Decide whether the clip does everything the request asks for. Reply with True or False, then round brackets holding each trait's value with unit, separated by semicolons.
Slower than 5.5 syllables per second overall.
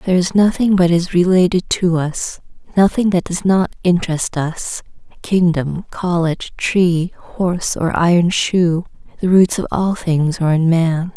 True (4.4 syllables/s)